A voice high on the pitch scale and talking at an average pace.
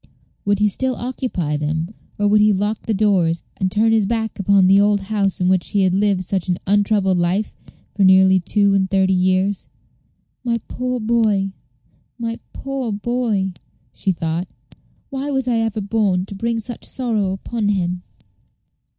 Yes: high, 200 Hz; average, 170 wpm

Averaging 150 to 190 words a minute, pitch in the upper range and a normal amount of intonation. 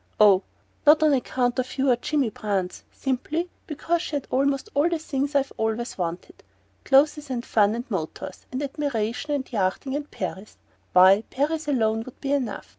Yes: average, 175 wpm; very high, 260 Hz; average, 4.7 semitones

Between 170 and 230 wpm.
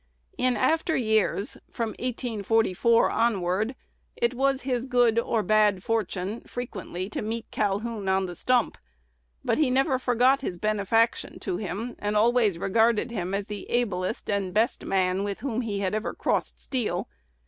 No: average, 155 wpm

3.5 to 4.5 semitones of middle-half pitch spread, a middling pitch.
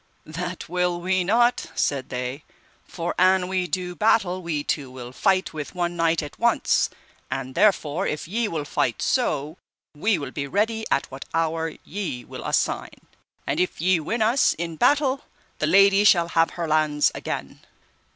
Yes: average, 4.2 semitones; medium, 170 Hz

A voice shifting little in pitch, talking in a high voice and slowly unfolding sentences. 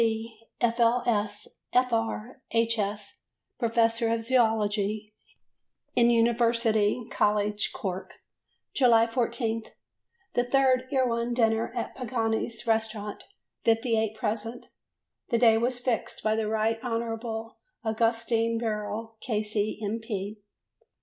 Yes: narrow, 1.4 semitones; high, 225 Hz; slow, 95 wpm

